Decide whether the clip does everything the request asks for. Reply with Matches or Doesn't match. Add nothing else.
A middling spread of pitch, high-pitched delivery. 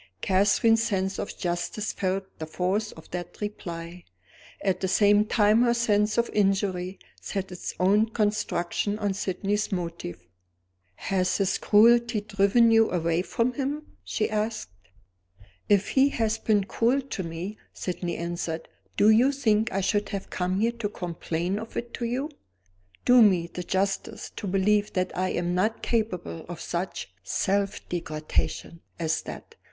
Matches